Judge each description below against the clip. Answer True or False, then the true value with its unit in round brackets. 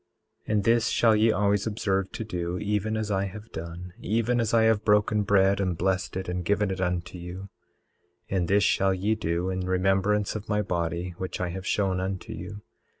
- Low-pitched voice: True (95 Hz)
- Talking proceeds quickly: True (210 wpm)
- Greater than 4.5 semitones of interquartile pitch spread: False (2.4 semitones)